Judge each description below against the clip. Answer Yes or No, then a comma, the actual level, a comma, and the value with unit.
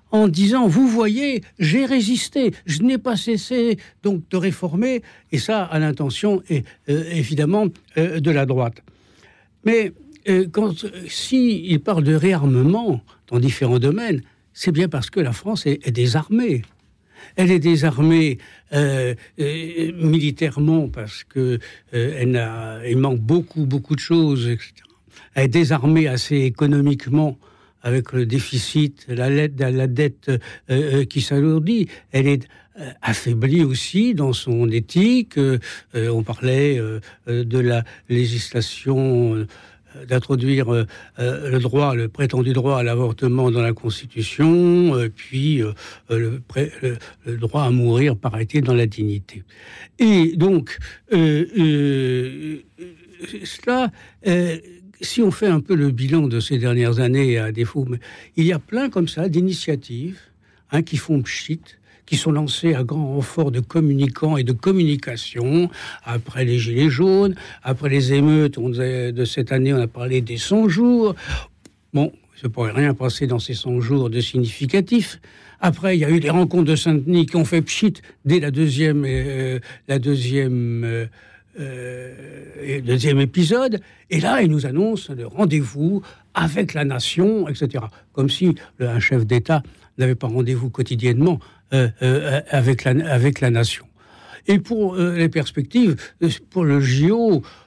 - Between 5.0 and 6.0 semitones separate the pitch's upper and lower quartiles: Yes, average, 5.3 semitones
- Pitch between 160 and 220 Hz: No, medium, 140 Hz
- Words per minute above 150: No, slow, 145 wpm